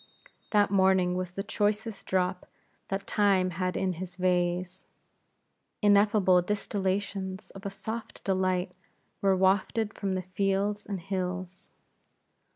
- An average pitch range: No, narrow, 1.6 semitones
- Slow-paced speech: Yes, slow, 120 wpm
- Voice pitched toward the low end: No, high, 190 Hz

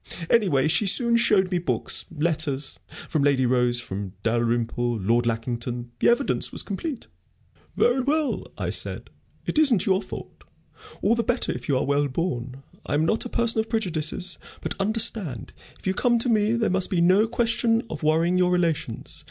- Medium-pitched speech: Yes, medium, 175 Hz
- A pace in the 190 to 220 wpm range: No, average, 175 wpm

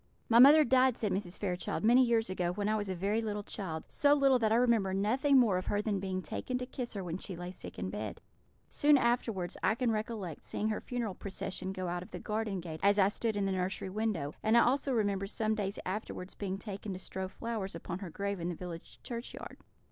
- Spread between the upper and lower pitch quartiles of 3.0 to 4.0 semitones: Yes, average, 3.7 semitones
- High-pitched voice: Yes, high, 205 Hz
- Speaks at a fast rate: Yes, fast, 235 wpm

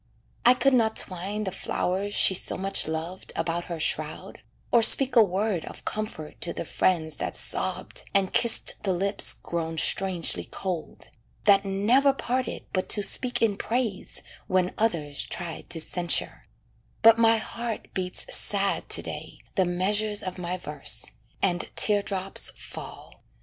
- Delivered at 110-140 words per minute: No, average, 155 wpm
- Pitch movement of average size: Yes, average, 3.8 semitones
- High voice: Yes, high, 195 Hz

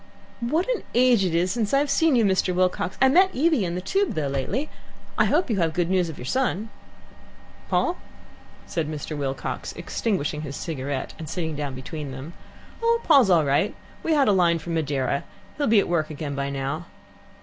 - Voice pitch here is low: No, medium, 175 Hz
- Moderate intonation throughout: No, wide, 8.5 semitones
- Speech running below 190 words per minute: No, average, 195 wpm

